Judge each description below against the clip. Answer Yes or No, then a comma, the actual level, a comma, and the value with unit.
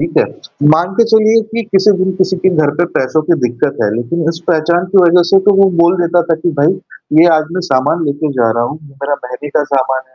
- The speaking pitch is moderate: Yes, medium, 165 Hz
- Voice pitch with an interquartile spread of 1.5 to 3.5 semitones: No, average, 4.8 semitones